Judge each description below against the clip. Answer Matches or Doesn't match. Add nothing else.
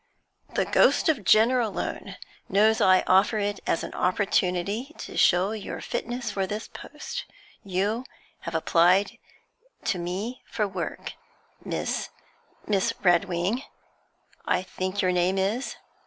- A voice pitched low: Doesn't match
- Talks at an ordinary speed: Doesn't match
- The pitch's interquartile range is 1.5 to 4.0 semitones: Matches